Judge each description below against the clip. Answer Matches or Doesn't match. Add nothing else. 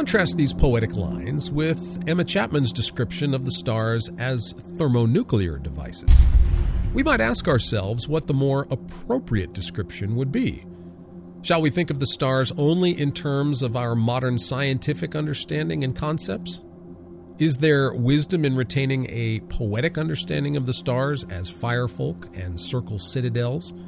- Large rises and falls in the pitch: Matches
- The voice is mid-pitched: Doesn't match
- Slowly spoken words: Doesn't match